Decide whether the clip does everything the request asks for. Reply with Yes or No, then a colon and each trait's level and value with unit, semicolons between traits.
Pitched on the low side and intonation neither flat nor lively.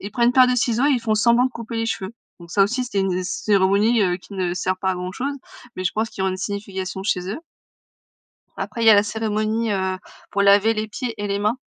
No: high, 205 Hz; average, 3.2 semitones